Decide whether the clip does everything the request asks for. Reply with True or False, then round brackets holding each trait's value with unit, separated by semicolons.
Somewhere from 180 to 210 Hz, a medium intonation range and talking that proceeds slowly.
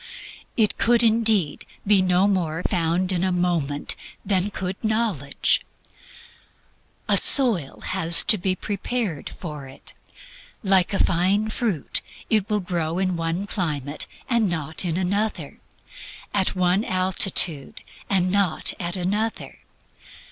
True (185 Hz; 3.4 semitones; 125 wpm)